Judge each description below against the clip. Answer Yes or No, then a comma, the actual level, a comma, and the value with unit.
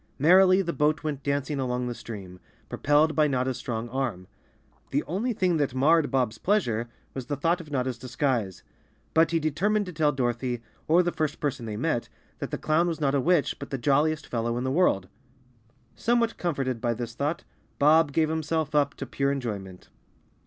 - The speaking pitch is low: No, medium, 145 Hz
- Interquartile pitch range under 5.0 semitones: Yes, average, 4.5 semitones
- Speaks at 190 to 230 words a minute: Yes, average, 195 wpm